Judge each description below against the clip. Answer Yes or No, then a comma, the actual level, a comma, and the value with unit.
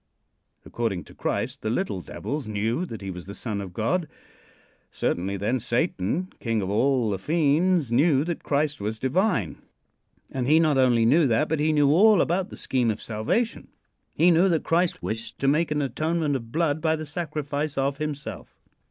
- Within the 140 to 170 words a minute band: No, average, 185 wpm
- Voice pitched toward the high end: No, medium, 140 Hz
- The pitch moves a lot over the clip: Yes, wide, 6.1 semitones